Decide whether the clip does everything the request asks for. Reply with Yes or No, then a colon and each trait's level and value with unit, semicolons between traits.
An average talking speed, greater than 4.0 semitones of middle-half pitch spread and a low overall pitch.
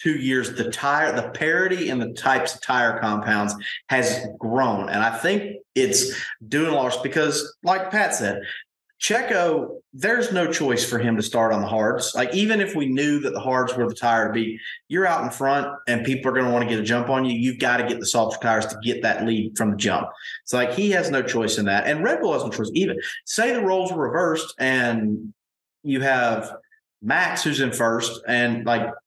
No: fast, 225 wpm; average, 4.7 semitones; low, 125 Hz